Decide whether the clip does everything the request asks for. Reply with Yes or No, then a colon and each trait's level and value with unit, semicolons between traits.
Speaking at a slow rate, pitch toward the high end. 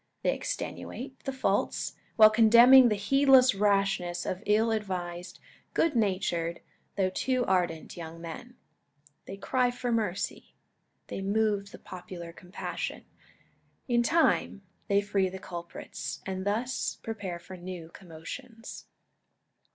Yes: slow, 120 wpm; high, 200 Hz